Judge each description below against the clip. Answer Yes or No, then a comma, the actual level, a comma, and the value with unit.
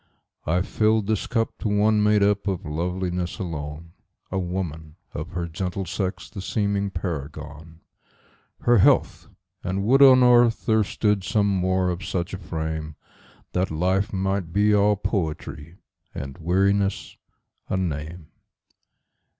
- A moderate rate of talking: No, slow, 125 wpm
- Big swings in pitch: No, average, 3.6 semitones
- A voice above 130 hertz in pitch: No, very low, 95 Hz